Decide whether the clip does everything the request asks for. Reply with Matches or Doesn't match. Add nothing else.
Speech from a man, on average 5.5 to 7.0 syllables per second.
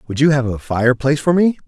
Matches